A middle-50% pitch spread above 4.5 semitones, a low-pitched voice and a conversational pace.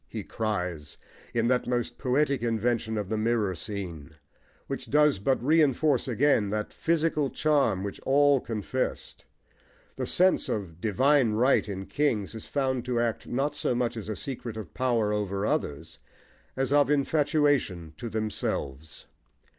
Yes: average, 5.2 semitones; low, 120 Hz; average, 145 wpm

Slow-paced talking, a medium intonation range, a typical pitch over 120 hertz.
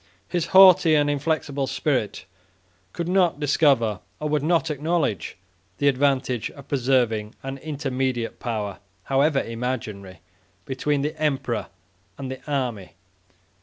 Yes: slow, 120 wpm; average, 3.5 semitones; low, 135 Hz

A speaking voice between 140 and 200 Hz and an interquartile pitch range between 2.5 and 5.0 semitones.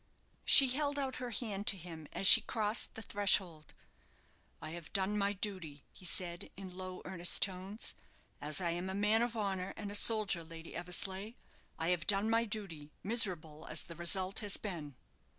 Yes: high, 190 Hz; average, 3.5 semitones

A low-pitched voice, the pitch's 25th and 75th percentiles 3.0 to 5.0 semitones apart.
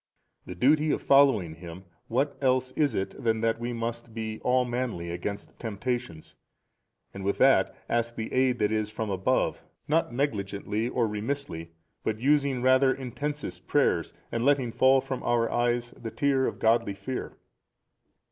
Yes: low, 120 Hz; average, 3.7 semitones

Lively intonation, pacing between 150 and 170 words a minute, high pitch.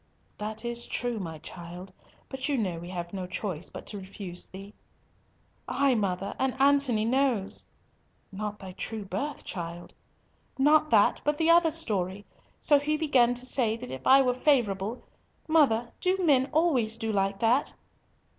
Yes: wide, 6.0 semitones; average, 155 wpm; high, 225 Hz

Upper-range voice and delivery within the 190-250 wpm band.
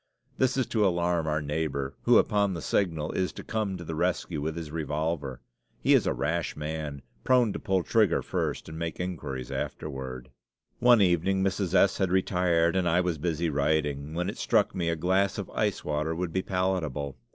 No: very low, 85 Hz; average, 195 wpm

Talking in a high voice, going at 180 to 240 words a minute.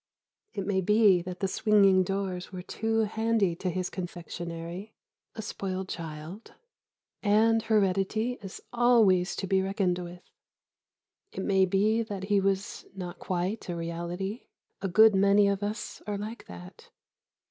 No: high, 195 Hz; average, 145 wpm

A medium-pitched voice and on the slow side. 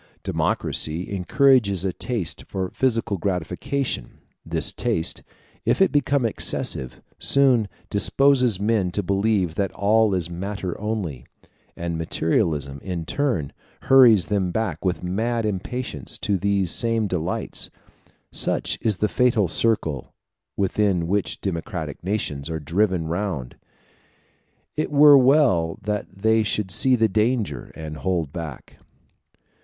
No: low, 100 Hz; slow, 125 wpm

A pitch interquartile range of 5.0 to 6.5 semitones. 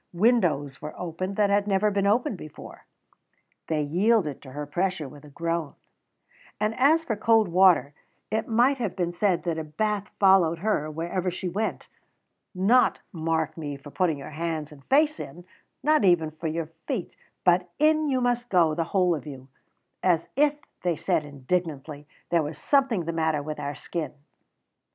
Yes: average, 5.3 semitones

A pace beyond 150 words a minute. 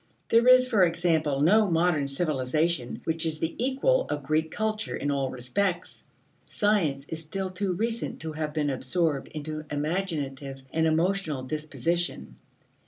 No: average, 145 wpm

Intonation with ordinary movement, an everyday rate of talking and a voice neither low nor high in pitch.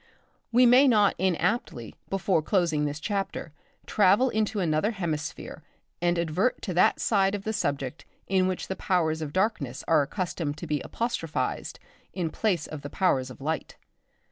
Yes: average, 4.7 semitones; average, 160 wpm; medium, 180 Hz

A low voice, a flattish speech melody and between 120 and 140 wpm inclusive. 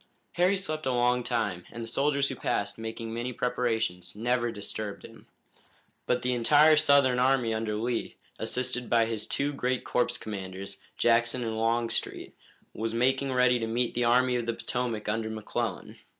No: low, 120 Hz; narrow, 2.1 semitones; average, 165 wpm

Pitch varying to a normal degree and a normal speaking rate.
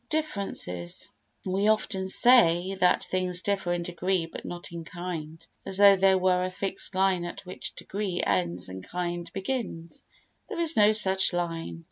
No: narrow, 2.2 semitones; average, 160 wpm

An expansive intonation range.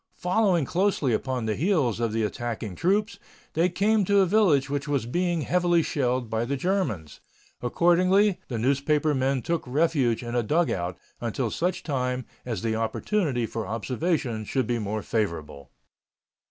Yes: wide, 7.2 semitones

